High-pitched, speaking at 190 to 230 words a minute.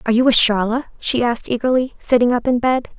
Yes: high, 240 Hz; average, 200 wpm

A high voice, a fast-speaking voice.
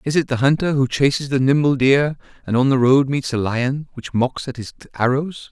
No: low, 135 Hz; fast, 230 wpm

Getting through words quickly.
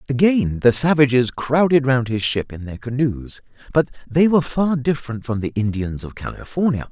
No: average, 175 wpm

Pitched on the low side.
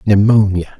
Yes: low, 100 Hz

